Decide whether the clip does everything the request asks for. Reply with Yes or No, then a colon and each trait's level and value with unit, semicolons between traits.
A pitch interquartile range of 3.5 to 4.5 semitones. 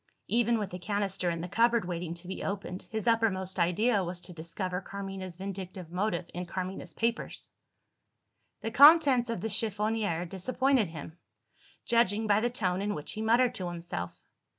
Yes: average, 4.0 semitones